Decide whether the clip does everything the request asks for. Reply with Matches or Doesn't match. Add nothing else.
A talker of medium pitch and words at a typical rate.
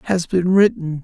Matches